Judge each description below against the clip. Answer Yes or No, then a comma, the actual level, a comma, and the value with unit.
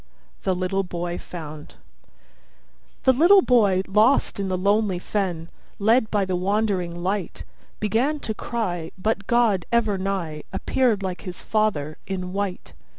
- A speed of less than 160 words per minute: Yes, average, 140 wpm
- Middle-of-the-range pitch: No, high, 195 Hz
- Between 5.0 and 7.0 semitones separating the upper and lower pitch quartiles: No, average, 3.2 semitones